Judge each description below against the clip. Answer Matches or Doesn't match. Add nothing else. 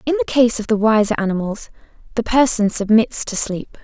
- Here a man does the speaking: Doesn't match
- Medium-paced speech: Matches